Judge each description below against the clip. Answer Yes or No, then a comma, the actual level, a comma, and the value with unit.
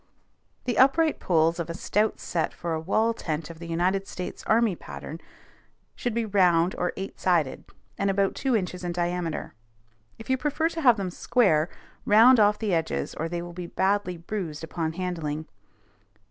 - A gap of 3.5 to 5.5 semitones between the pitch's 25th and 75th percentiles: Yes, average, 4.5 semitones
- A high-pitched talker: No, medium, 180 Hz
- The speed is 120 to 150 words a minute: No, average, 175 wpm